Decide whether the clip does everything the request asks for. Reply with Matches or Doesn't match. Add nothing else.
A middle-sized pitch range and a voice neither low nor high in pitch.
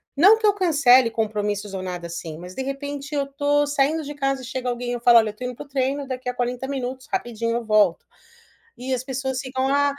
Doesn't match